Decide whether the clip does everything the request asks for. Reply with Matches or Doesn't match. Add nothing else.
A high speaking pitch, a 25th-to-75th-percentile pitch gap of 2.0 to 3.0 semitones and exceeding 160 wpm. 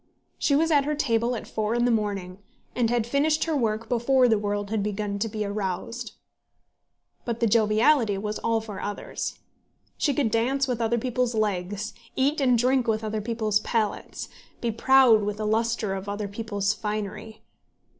Matches